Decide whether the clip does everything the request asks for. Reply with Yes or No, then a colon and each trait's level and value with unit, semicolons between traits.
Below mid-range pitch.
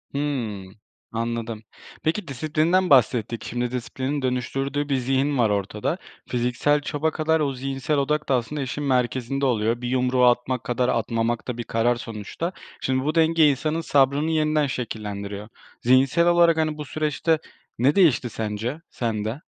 Yes: low, 130 Hz